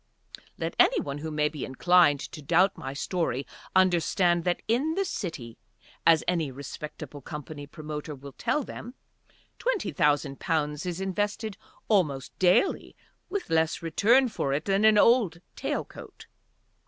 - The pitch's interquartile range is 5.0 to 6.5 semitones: Yes, wide, 5.6 semitones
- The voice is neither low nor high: Yes, medium, 170 Hz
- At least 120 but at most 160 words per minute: Yes, average, 140 wpm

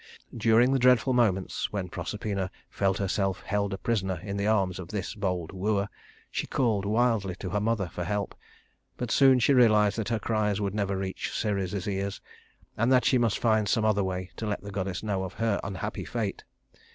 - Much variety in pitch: No, narrow, 2.5 semitones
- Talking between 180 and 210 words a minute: Yes, average, 195 wpm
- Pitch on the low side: Yes, low, 100 Hz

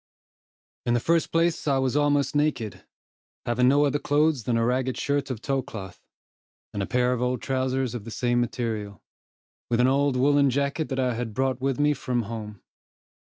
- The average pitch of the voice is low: Yes, low, 130 Hz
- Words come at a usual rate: Yes, average, 190 wpm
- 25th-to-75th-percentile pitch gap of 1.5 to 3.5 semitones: Yes, average, 3.0 semitones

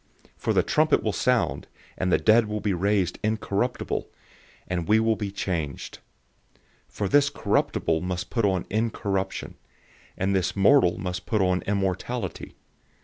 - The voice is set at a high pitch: No, low, 100 Hz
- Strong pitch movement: No, average, 3.2 semitones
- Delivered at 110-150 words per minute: Yes, average, 145 wpm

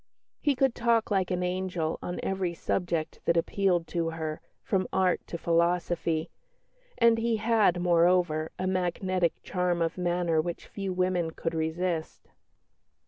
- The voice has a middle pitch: Yes, medium, 180 Hz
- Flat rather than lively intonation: Yes, narrow, 1.9 semitones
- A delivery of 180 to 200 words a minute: No, average, 140 wpm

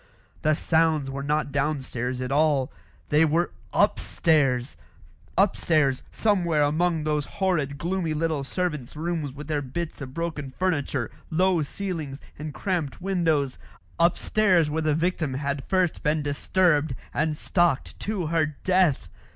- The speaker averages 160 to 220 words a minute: No, slow, 135 wpm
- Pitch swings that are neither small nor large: Yes, average, 3.3 semitones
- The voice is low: No, medium, 155 Hz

